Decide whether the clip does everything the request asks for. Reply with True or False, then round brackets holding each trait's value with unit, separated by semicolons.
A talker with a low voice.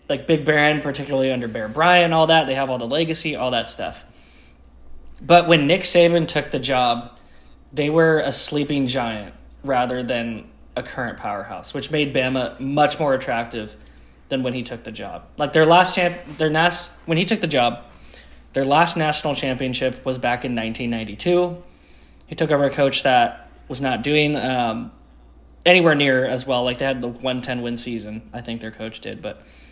True (130 Hz)